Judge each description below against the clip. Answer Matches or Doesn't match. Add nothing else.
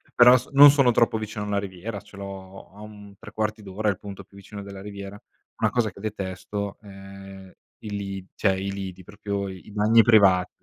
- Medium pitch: Doesn't match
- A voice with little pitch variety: Matches